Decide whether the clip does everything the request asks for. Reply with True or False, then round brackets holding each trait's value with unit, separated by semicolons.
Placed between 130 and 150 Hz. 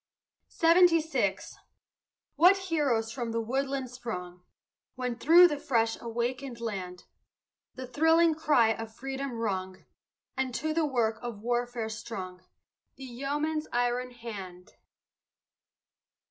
False (245 Hz)